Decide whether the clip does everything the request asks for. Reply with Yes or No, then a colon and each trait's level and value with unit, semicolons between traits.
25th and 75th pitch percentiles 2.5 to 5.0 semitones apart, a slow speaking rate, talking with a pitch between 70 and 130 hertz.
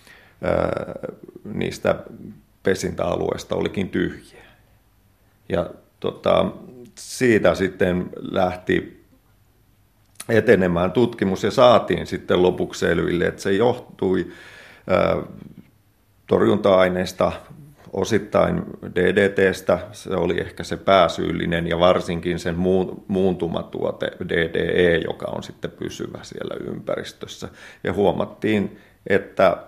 Yes: average, 2.8 semitones; slow, 85 wpm; very low, 95 Hz